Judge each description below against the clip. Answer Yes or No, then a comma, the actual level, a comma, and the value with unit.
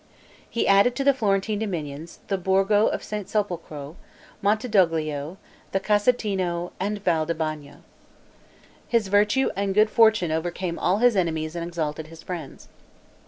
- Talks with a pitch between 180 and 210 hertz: Yes, high, 190 Hz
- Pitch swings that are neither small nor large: Yes, average, 4.3 semitones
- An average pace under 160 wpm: Yes, average, 140 wpm